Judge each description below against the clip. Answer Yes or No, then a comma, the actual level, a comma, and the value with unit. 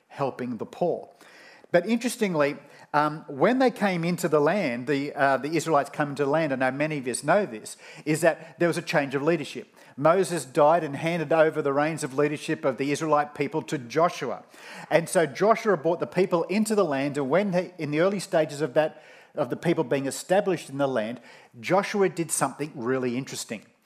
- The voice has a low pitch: No, medium, 155 Hz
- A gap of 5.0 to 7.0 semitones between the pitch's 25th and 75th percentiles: No, average, 3.3 semitones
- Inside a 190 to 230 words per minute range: Yes, average, 200 wpm